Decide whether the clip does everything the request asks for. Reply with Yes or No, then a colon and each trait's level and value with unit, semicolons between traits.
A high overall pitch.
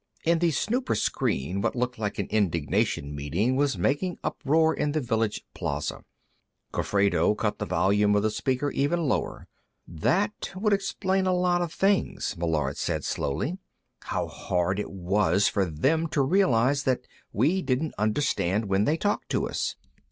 No: low, 125 Hz